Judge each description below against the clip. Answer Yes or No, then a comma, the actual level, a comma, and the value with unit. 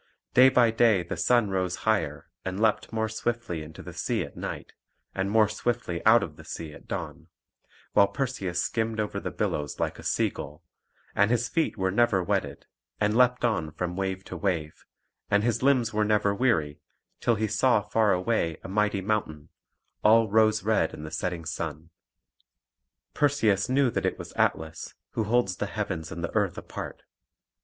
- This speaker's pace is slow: No, average, 180 wpm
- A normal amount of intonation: Yes, average, 4.2 semitones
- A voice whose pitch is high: No, low, 105 Hz